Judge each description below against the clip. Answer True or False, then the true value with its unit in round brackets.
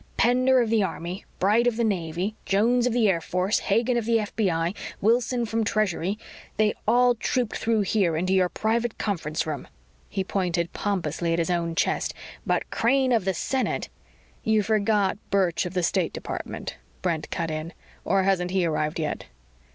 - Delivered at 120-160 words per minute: False (175 wpm)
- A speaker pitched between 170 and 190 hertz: False (200 Hz)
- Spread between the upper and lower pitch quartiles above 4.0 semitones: True (4.6 semitones)